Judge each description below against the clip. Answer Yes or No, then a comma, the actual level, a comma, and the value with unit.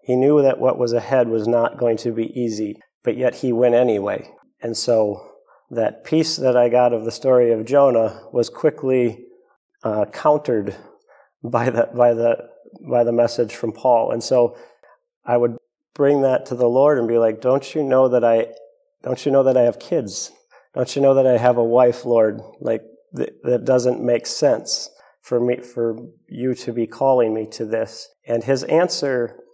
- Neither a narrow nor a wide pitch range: No, narrow, 2.0 semitones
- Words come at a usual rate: Yes, average, 190 wpm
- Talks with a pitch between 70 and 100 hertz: No, low, 120 Hz